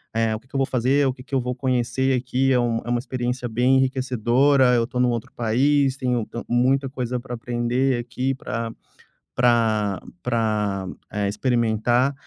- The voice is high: No, low, 125 Hz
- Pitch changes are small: Yes, narrow, 2.0 semitones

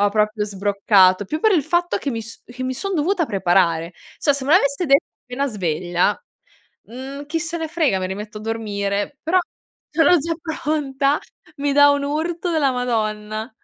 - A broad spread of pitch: Yes, wide, 6.7 semitones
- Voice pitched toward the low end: No, very high, 260 Hz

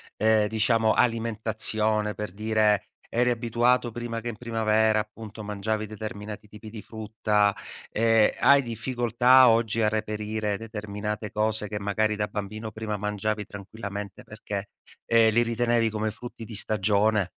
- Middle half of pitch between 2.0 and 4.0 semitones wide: No, narrow, 1.4 semitones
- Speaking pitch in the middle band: No, low, 110 Hz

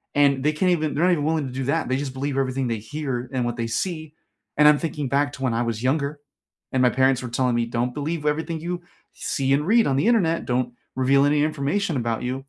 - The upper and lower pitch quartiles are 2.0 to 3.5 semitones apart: Yes, average, 3.2 semitones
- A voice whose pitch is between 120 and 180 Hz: Yes, medium, 140 Hz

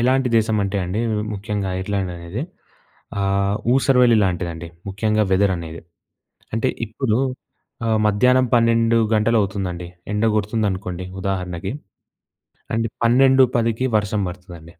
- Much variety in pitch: No, average, 3.6 semitones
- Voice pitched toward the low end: Yes, low, 105 Hz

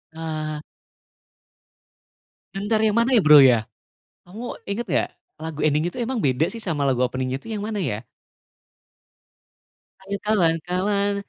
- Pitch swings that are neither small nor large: No, wide, 5.8 semitones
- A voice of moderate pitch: Yes, medium, 170 Hz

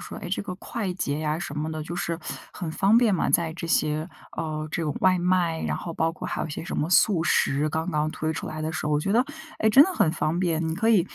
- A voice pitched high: No, medium, 165 Hz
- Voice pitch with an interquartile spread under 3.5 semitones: Yes, average, 2.9 semitones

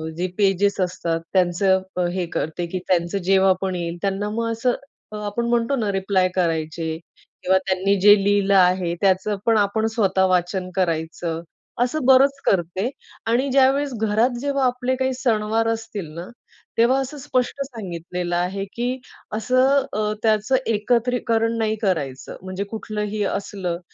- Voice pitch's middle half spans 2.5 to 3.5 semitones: No, average, 4.1 semitones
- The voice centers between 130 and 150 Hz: No, high, 205 Hz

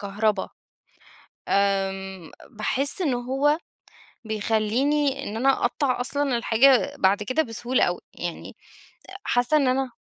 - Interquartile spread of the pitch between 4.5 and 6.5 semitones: Yes, average, 4.8 semitones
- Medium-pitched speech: No, high, 245 Hz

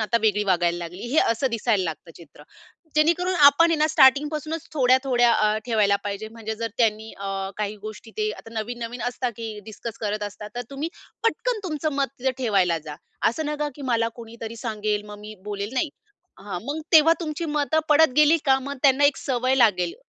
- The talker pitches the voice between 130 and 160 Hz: No, high, 230 Hz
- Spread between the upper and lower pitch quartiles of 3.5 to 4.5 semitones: No, wide, 5.4 semitones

